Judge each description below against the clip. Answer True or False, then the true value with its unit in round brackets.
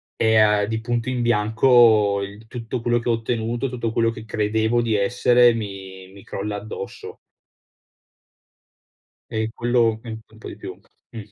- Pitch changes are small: True (2.1 semitones)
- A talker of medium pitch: False (110 Hz)